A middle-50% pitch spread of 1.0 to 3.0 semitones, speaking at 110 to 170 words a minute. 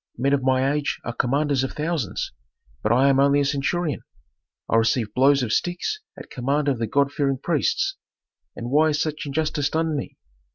No: average, 2.7 semitones; average, 190 wpm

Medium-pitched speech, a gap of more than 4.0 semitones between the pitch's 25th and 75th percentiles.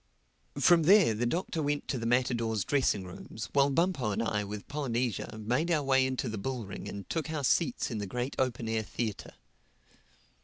No: low, 125 Hz; average, 4.6 semitones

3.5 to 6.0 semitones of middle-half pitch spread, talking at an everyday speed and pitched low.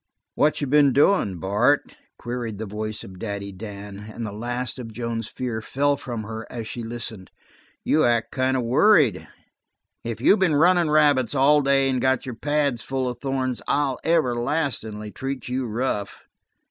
Yes: average, 3.9 semitones; average, 170 wpm; low, 125 Hz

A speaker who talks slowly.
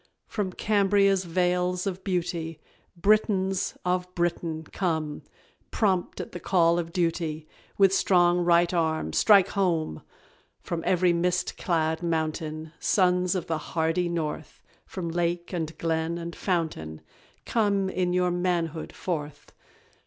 Yes: slow, 125 wpm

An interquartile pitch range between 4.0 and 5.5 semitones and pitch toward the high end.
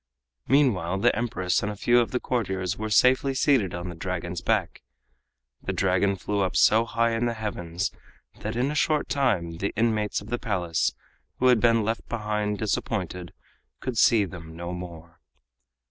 No: average, 4.5 semitones; low, 105 Hz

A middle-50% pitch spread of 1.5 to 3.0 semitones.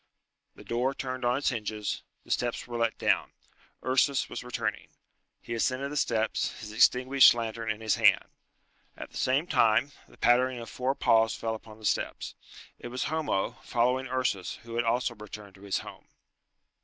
Yes: narrow, 2.5 semitones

